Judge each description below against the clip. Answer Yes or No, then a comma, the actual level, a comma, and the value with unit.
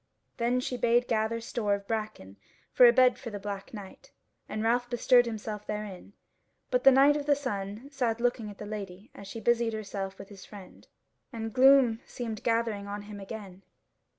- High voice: Yes, high, 225 Hz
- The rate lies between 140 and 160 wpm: No, average, 185 wpm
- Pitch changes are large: No, average, 3.0 semitones